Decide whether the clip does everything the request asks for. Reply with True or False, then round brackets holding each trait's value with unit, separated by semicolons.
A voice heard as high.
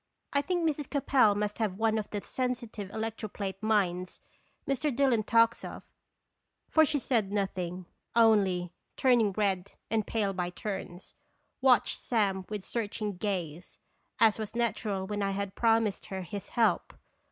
True (210 Hz)